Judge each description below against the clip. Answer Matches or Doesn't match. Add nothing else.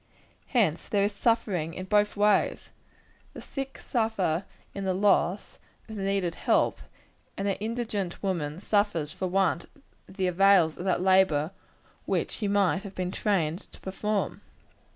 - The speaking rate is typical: Matches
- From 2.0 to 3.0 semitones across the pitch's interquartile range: Matches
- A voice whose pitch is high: Matches